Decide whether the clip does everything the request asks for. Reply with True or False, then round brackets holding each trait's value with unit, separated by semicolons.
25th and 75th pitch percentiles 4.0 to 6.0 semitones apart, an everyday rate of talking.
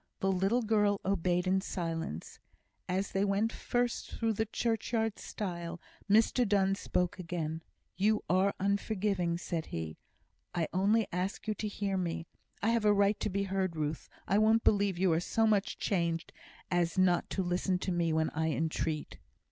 False (3.2 semitones; 170 wpm)